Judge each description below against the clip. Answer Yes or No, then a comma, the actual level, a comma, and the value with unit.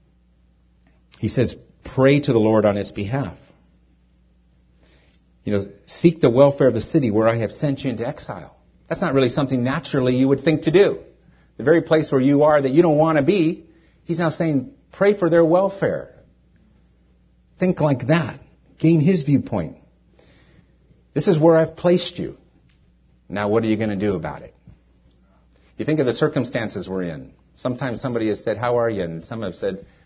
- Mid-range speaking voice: No, low, 130 Hz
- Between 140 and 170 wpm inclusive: No, average, 185 wpm